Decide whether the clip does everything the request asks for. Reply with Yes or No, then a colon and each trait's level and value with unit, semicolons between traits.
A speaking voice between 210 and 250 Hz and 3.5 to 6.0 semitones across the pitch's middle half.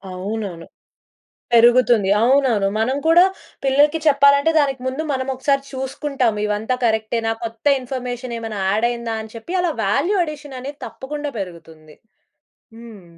Yes: high, 245 Hz; average, 4.0 semitones